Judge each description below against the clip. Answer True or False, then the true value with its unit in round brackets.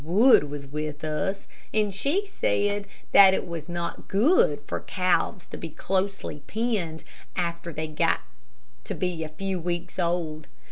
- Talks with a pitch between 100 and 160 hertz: False (175 Hz)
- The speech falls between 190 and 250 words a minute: False (150 wpm)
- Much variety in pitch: False (4.0 semitones)